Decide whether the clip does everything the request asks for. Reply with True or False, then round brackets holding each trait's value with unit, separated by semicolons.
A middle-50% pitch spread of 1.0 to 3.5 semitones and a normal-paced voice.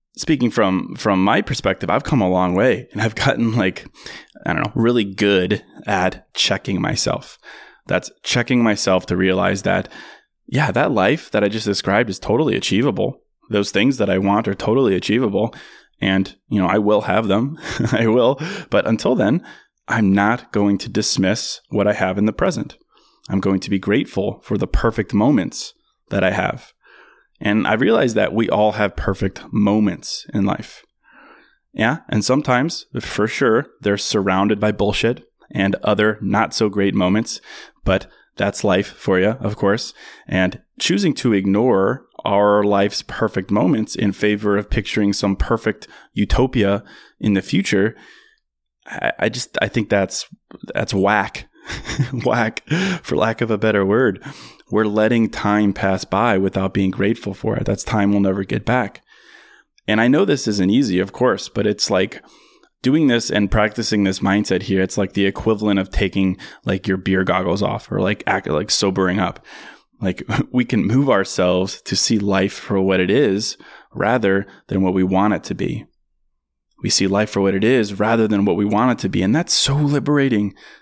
True (2.4 semitones; 175 wpm)